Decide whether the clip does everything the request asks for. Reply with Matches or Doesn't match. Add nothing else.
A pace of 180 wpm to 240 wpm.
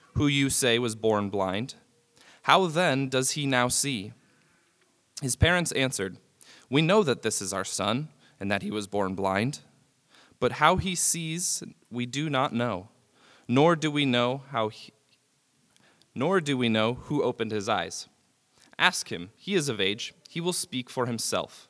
Doesn't match